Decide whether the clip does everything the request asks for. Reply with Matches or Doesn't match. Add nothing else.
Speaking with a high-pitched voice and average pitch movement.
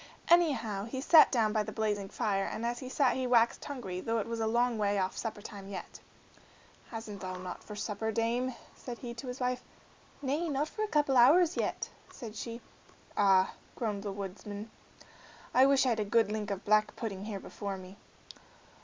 Matches